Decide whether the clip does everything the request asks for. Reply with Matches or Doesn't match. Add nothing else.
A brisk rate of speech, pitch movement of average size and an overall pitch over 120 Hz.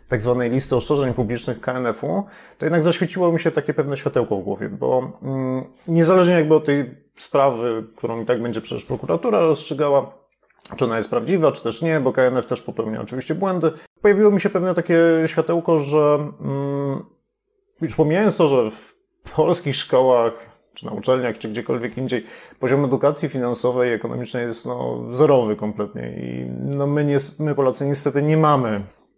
Matches